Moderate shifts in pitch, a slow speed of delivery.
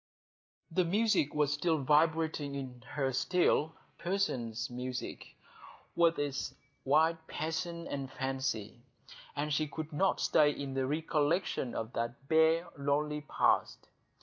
Yes: average, 3.3 semitones; slow, 110 wpm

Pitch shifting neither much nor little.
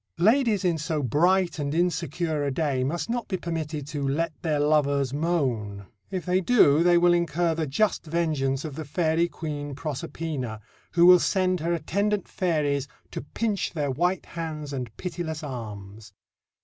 Yes: average, 3.6 semitones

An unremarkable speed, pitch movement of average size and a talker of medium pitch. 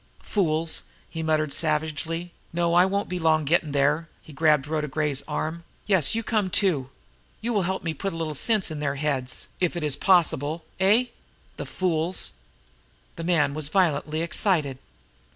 Yes: average, 170 wpm; average, 3.1 semitones; medium, 160 Hz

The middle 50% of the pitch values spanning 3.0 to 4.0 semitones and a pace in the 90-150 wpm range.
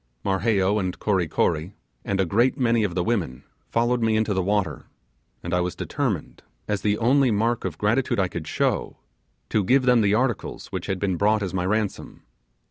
No: average, 3.7 semitones; average, 195 wpm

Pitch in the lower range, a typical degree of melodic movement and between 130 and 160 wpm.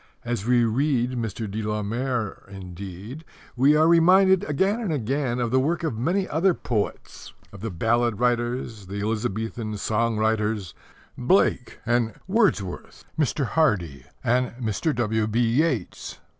Yes: low, 120 Hz; average, 4.8 semitones; average, 140 wpm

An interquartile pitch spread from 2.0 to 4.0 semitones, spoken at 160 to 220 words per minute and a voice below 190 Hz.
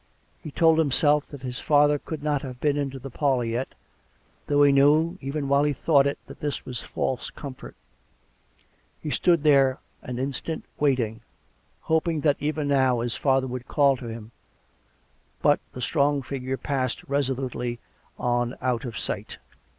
Yes: narrow, 2.5 semitones; average, 165 wpm; medium, 140 Hz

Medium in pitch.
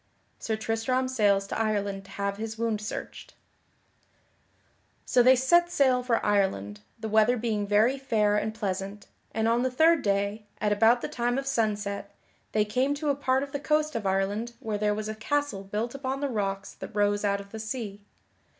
No: high, 220 Hz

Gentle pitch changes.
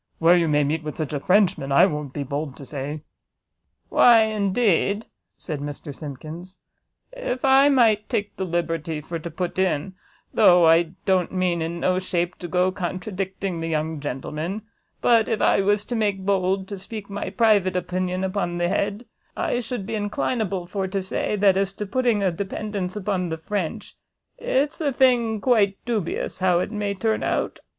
No: average, 3.7 semitones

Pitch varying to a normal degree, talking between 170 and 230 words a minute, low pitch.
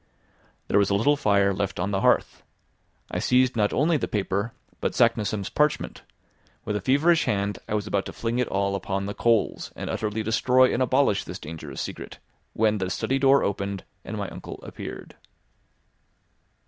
Yes: average, 4.3 semitones; average, 175 wpm; low, 105 Hz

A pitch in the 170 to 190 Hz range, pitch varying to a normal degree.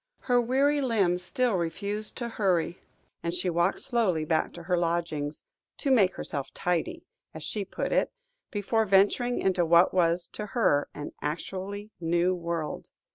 Yes: medium, 185 Hz; average, 4.0 semitones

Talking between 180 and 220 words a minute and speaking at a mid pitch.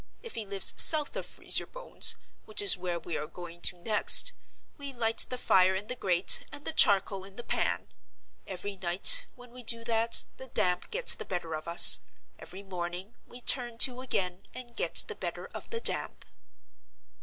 No: average, 185 wpm; high, 205 Hz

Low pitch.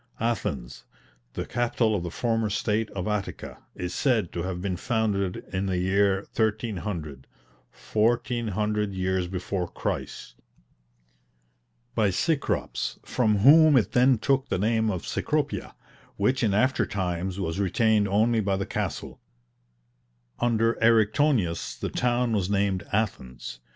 Yes: low, 105 Hz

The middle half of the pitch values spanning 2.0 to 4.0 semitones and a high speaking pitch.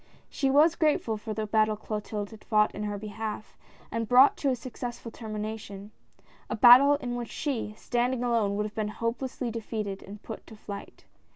Yes: narrow, 2.5 semitones; high, 220 Hz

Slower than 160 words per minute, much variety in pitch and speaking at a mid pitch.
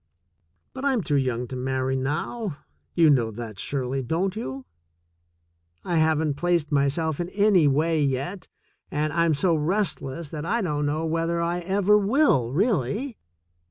No: average, 150 wpm; average, 4.7 semitones; medium, 160 Hz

